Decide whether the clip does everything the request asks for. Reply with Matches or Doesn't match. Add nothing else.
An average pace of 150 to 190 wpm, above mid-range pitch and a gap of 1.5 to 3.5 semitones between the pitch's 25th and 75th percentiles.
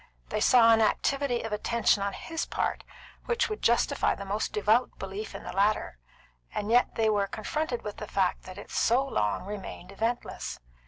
Matches